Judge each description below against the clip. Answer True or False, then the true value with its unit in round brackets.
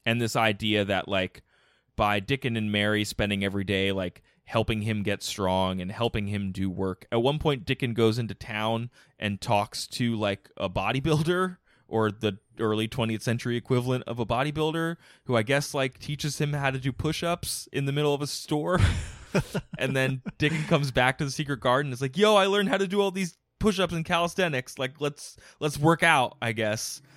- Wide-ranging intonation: True (5.8 semitones)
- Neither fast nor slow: True (195 wpm)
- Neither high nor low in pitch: False (125 Hz)